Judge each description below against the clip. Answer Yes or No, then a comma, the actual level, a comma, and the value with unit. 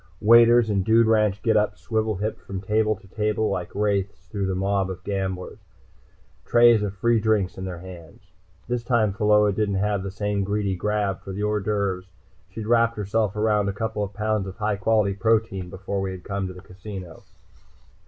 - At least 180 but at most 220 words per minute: Yes, average, 185 wpm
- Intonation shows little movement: Yes, narrow, 2.1 semitones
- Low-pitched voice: Yes, low, 105 Hz